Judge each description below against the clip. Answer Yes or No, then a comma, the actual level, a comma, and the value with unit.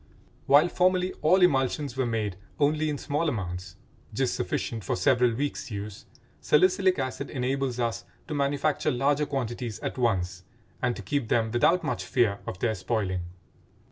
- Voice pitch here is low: Yes, low, 130 Hz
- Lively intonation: No, average, 4.7 semitones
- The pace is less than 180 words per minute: Yes, average, 155 wpm